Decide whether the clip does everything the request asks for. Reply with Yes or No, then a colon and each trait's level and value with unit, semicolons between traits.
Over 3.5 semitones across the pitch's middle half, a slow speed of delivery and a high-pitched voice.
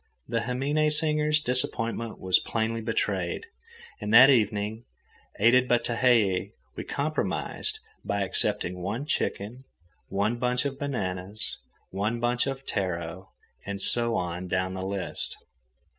No: average, 4.5 semitones; slow, 125 wpm; low, 115 Hz